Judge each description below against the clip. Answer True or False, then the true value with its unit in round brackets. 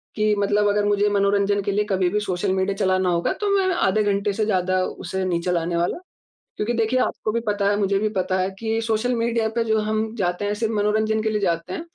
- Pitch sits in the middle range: False (205 Hz)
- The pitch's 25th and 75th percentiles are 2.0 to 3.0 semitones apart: True (2.5 semitones)